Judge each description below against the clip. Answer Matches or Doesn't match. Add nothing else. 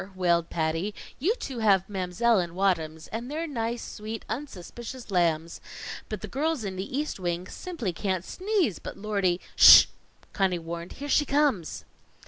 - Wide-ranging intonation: Matches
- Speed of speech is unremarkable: Matches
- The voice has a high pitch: Matches